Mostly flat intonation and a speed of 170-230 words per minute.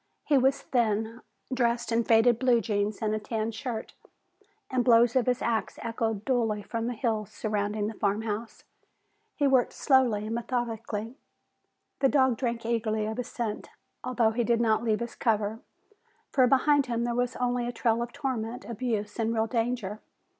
Yes: narrow, 2.0 semitones; average, 175 wpm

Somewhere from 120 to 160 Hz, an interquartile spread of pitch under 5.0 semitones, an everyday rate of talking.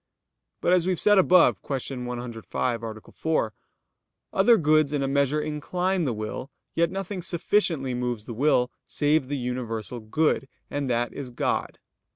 No: medium, 140 Hz; average, 5.3 semitones; average, 160 wpm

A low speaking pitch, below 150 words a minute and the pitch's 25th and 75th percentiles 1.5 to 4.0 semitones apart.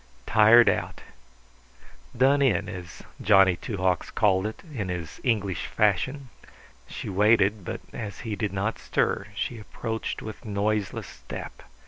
Yes: low, 105 Hz; slow, 135 wpm; average, 2.8 semitones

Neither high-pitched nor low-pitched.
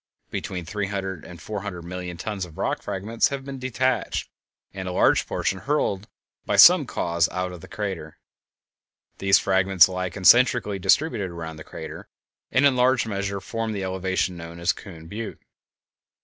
No: very low, 95 Hz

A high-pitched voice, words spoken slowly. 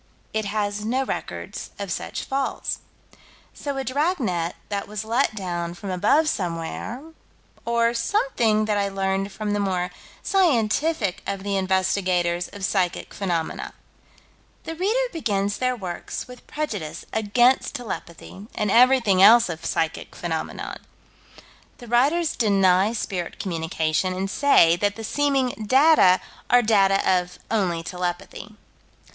Yes: high, 205 Hz; slow, 130 wpm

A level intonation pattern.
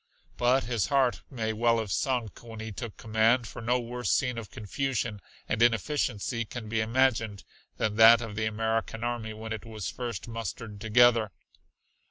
Yes: narrow, 1.7 semitones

